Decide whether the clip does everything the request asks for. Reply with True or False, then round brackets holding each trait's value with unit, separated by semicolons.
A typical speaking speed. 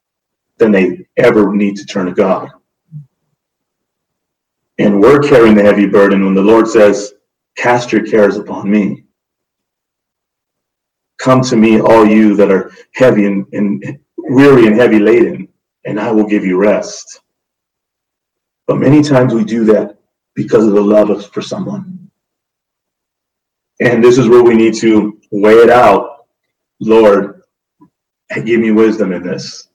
True (145 wpm)